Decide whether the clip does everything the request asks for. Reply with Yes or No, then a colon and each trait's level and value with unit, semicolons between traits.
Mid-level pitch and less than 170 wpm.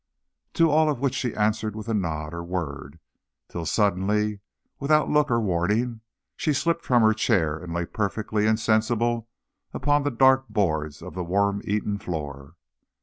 No: low, 105 Hz; average, 160 wpm